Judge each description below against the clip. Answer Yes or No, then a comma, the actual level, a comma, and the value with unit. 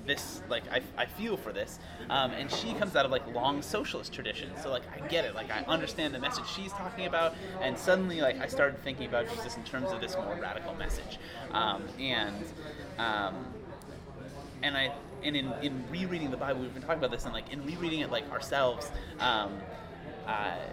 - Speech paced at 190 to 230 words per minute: Yes, fast, 205 wpm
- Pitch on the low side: No, medium, 150 Hz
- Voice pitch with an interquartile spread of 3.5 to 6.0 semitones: Yes, average, 4.7 semitones